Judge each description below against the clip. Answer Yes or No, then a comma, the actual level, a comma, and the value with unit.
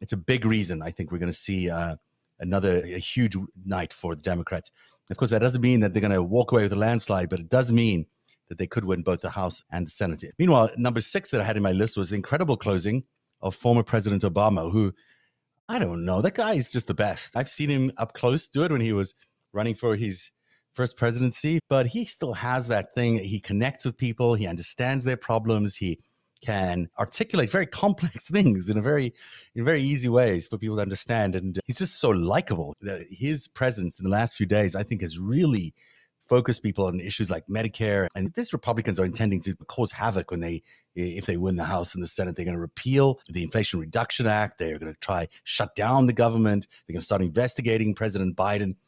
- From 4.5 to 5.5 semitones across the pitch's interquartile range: Yes, average, 4.8 semitones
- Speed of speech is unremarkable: No, fast, 225 wpm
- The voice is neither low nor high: No, low, 105 Hz